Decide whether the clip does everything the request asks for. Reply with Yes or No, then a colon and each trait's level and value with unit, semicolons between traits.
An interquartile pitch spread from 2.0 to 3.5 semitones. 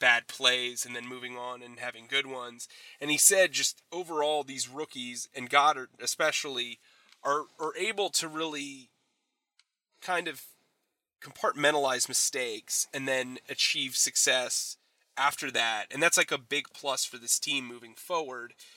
Yes: average, 3.2 semitones